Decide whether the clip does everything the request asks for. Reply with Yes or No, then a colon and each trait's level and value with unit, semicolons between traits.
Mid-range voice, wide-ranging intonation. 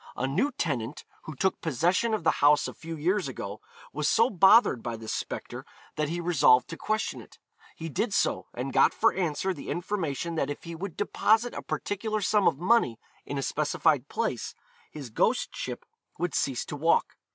Yes: medium, 165 Hz; wide, 6.0 semitones